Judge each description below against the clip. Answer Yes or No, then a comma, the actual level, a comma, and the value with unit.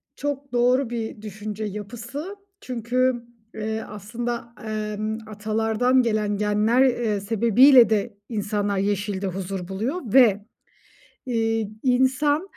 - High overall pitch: Yes, high, 220 Hz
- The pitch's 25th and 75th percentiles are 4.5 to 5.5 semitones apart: No, average, 3.0 semitones